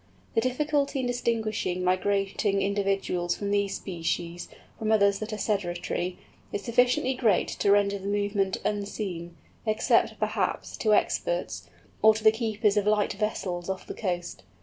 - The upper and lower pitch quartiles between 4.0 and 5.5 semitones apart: No, average, 2.8 semitones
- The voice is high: Yes, high, 200 Hz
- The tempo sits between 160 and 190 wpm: No, average, 150 wpm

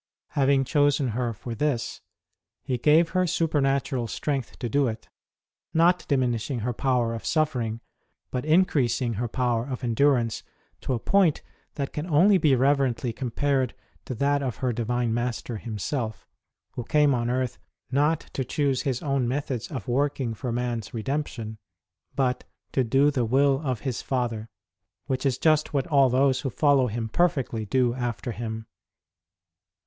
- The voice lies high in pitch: No, low, 130 Hz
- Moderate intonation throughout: Yes, average, 3.2 semitones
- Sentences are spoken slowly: No, average, 160 wpm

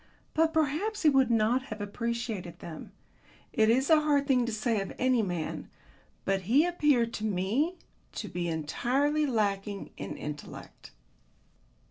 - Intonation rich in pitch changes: Yes, wide, 6.2 semitones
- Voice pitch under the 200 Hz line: No, high, 235 Hz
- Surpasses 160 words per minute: No, average, 145 wpm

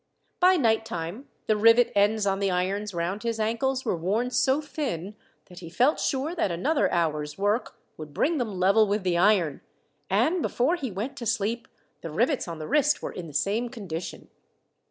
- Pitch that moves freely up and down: Yes, wide, 5.7 semitones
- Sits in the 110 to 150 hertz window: No, high, 215 Hz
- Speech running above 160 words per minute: Yes, average, 185 wpm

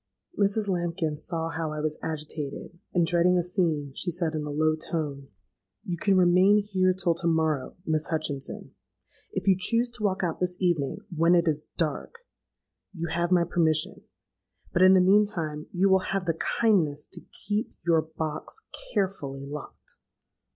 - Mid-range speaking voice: Yes, medium, 170 Hz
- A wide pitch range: No, average, 3.2 semitones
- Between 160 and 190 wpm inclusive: Yes, average, 165 wpm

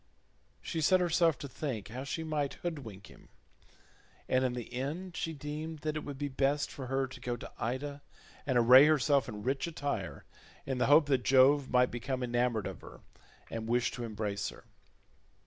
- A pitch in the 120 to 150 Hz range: Yes, low, 135 Hz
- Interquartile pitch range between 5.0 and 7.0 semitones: No, average, 3.3 semitones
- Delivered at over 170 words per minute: Yes, average, 185 wpm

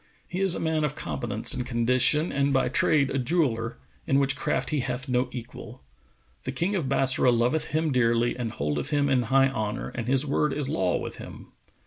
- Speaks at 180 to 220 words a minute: Yes, average, 200 wpm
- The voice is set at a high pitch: No, low, 130 Hz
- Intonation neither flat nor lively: Yes, average, 3.3 semitones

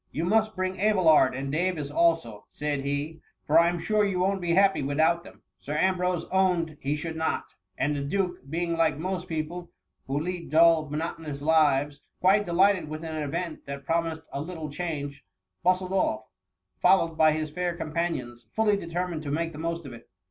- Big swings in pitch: No, average, 3.2 semitones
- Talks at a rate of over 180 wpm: Yes, average, 190 wpm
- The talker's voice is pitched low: No, medium, 165 Hz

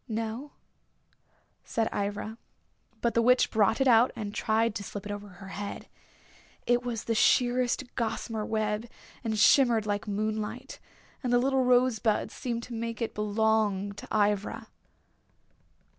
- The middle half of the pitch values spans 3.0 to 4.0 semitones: No, narrow, 2.5 semitones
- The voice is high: Yes, high, 220 Hz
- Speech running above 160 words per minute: No, average, 140 wpm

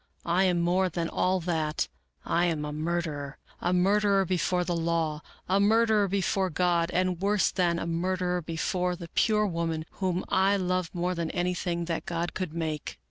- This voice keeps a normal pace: Yes, average, 180 wpm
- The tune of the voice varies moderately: No, narrow, 1.9 semitones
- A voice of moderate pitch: Yes, medium, 175 Hz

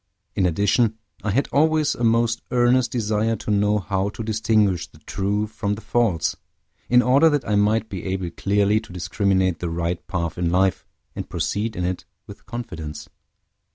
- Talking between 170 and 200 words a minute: Yes, average, 175 wpm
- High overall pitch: No, low, 105 Hz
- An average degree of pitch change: Yes, average, 3.6 semitones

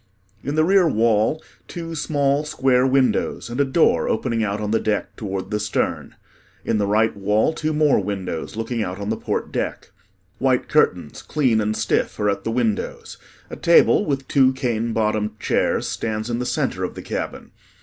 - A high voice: No, low, 115 Hz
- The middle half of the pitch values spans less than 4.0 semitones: No, average, 4.5 semitones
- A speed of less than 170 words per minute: No, average, 185 wpm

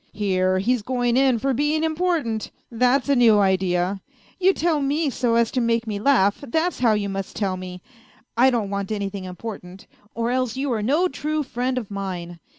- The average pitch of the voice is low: No, high, 230 Hz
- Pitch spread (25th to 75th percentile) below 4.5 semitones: No, average, 5.3 semitones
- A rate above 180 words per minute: Yes, average, 195 wpm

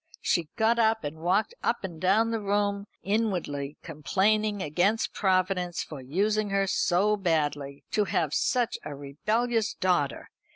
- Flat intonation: No, average, 5.0 semitones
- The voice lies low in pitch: No, high, 190 Hz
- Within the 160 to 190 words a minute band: No, average, 140 wpm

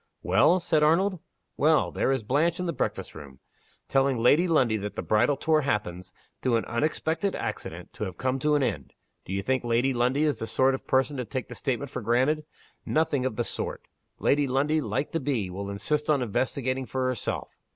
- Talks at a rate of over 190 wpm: Yes, fast, 205 wpm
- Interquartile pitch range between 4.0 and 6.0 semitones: Yes, average, 4.3 semitones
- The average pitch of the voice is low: Yes, low, 130 Hz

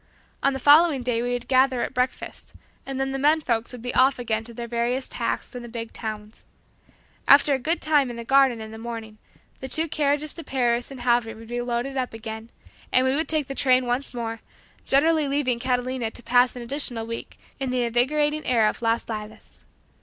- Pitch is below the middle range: No, very high, 250 Hz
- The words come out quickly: Yes, fast, 215 wpm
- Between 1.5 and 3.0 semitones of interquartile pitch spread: Yes, average, 2.7 semitones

